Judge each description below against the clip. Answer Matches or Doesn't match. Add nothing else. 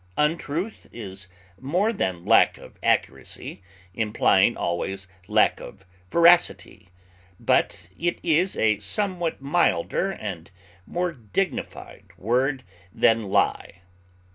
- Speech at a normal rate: Doesn't match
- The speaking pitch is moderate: Doesn't match